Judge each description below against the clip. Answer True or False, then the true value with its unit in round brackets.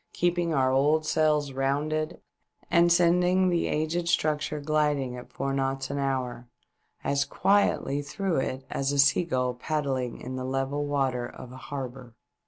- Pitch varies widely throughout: False (2.9 semitones)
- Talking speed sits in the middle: True (150 wpm)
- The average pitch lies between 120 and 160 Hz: True (140 Hz)